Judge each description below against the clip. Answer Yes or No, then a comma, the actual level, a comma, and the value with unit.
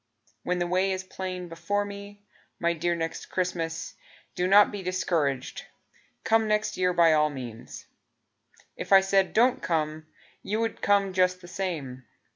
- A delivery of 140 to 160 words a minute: Yes, average, 155 wpm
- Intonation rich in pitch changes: No, average, 3.3 semitones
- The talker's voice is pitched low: No, medium, 180 Hz